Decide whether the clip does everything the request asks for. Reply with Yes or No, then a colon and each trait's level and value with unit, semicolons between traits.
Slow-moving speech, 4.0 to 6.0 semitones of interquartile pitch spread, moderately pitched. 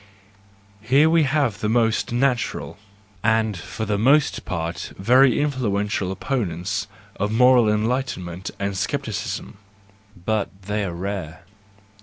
No: slow, 115 wpm; average, 4.3 semitones; low, 110 Hz